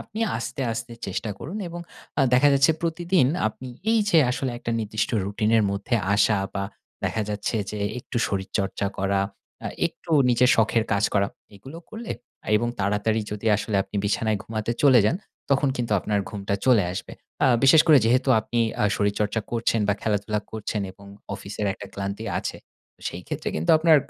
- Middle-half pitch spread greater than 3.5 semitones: Yes, average, 3.9 semitones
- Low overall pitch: Yes, low, 110 Hz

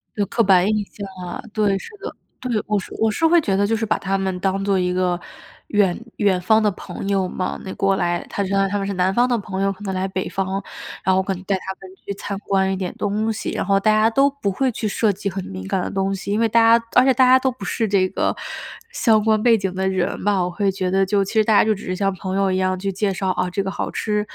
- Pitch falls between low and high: No, high, 195 Hz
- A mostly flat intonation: Yes, narrow, 2.2 semitones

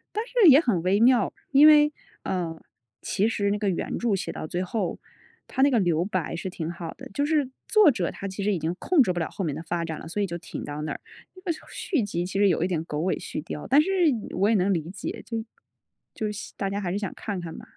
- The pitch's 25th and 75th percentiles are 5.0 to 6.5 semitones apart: Yes, wide, 5.4 semitones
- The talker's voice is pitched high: Yes, high, 195 Hz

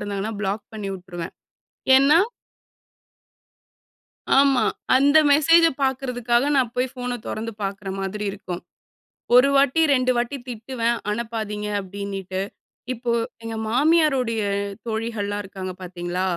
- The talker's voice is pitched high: Yes, high, 225 Hz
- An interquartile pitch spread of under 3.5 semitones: No, average, 4.2 semitones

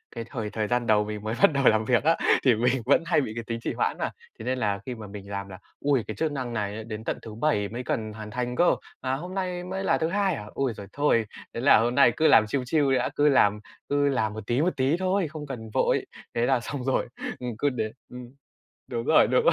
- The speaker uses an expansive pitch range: No, average, 4.7 semitones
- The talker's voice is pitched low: Yes, low, 125 Hz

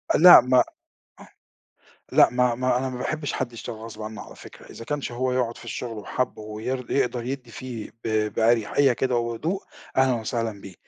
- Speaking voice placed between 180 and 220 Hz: No, low, 125 Hz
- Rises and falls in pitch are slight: Yes, narrow, 2.1 semitones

